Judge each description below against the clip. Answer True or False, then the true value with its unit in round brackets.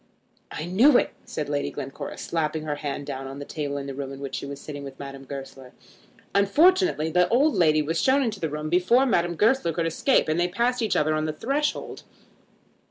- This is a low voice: False (155 Hz)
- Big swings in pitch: True (7.1 semitones)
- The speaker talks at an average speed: False (215 wpm)